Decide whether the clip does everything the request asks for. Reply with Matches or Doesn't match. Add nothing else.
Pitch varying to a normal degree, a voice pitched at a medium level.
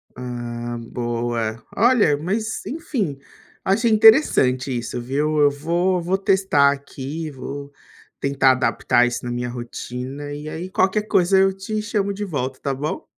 Doesn't match